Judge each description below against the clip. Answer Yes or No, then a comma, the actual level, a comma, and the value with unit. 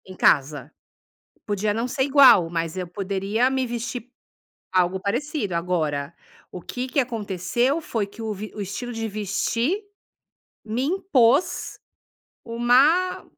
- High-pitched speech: Yes, high, 220 Hz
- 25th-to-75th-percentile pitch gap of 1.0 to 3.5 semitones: No, average, 5.2 semitones